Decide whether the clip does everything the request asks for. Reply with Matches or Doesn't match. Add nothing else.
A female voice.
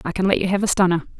Matches